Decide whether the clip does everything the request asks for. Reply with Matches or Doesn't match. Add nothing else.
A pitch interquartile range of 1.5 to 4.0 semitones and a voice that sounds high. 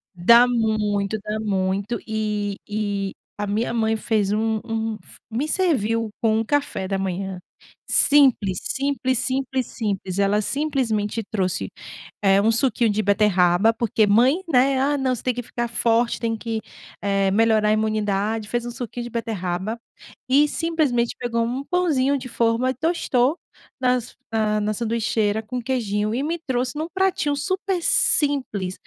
Matches